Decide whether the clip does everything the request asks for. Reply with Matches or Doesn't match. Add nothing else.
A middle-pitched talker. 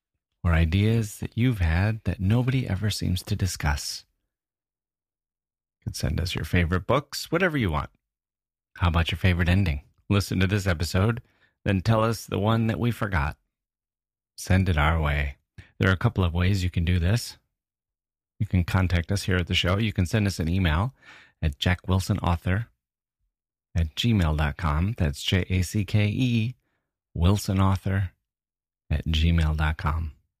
Doesn't match